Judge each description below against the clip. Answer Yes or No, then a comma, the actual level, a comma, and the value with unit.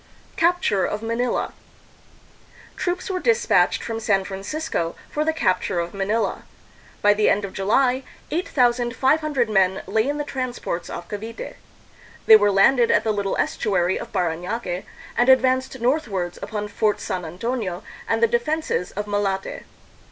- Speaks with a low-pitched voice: No, high, 220 Hz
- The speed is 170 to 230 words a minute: No, average, 150 wpm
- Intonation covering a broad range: No, average, 5.0 semitones